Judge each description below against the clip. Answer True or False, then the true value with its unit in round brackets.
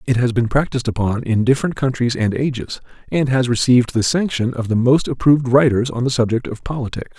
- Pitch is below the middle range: True (125 Hz)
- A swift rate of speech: True (210 wpm)